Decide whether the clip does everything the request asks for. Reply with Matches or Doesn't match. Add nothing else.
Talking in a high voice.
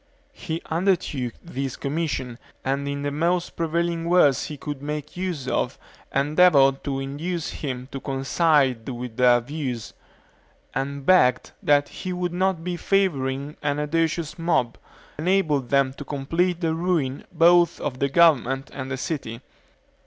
Doesn't match